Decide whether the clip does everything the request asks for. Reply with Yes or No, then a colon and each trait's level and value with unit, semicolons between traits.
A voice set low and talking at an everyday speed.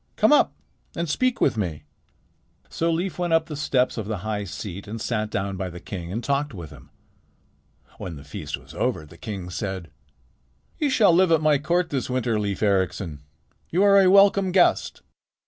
Yes: low, 115 Hz; average, 190 wpm